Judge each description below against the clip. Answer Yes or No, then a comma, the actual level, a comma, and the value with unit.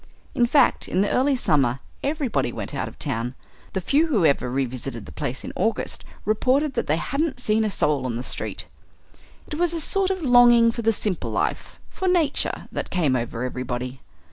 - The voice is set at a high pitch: Yes, high, 215 Hz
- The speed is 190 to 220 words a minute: Yes, average, 195 wpm